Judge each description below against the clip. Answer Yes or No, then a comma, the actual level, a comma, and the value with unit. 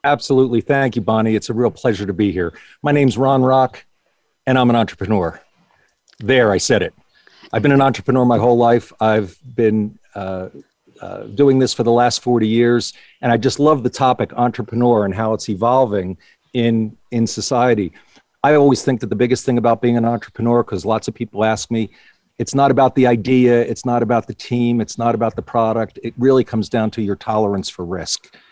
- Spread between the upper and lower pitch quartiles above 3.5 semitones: No, narrow, 2.5 semitones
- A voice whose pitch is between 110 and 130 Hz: Yes, low, 120 Hz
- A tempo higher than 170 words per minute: Yes, average, 200 wpm